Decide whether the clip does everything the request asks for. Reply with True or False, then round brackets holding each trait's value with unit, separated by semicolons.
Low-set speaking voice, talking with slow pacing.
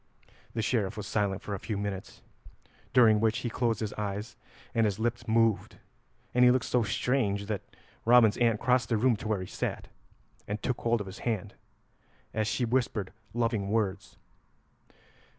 False (110 Hz; 170 wpm)